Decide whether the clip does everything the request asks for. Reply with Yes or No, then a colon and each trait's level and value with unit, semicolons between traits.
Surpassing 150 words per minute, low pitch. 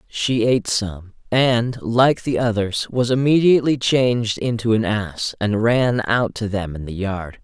Yes: average, 170 wpm; low, 115 Hz